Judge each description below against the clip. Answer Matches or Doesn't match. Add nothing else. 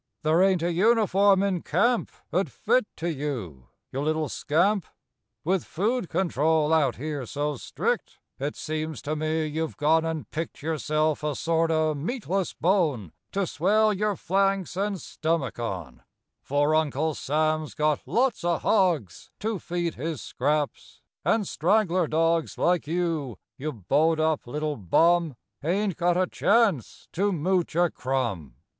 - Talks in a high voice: Doesn't match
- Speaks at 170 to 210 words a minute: Doesn't match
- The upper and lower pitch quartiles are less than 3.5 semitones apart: Doesn't match